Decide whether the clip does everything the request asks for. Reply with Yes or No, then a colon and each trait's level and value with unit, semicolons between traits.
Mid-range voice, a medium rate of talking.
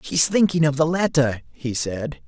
Yes: medium, 150 Hz; average, 185 wpm